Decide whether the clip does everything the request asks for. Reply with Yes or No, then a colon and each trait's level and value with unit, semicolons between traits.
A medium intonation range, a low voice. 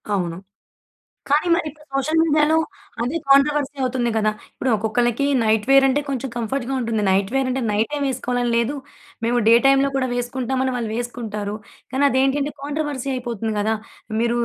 No: average, 3.2 semitones; very high, 255 Hz